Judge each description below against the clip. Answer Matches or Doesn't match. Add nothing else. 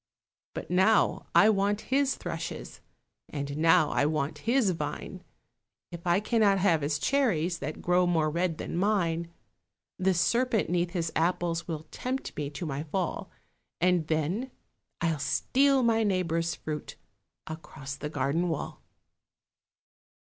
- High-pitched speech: Doesn't match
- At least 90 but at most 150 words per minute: Matches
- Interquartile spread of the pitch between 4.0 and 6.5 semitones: Matches